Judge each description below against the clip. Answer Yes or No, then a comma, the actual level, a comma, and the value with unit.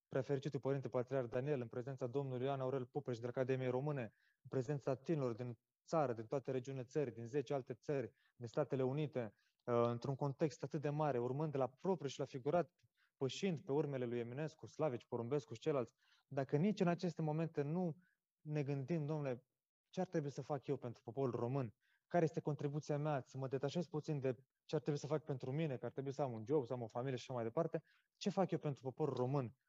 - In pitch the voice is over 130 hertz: Yes, medium, 140 Hz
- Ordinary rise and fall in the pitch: Yes, average, 3.1 semitones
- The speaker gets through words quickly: Yes, fast, 210 wpm